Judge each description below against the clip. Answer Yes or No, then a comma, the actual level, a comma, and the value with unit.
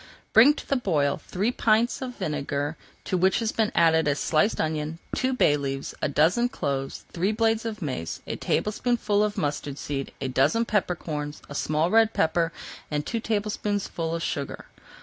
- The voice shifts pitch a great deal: Yes, wide, 6.9 semitones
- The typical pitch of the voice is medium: Yes, medium, 170 Hz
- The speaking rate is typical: Yes, average, 175 wpm